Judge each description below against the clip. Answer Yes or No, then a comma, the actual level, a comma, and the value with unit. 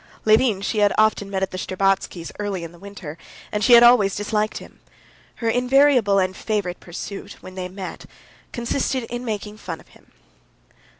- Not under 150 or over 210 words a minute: Yes, average, 175 wpm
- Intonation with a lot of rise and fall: No, average, 3.2 semitones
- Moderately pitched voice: No, high, 205 Hz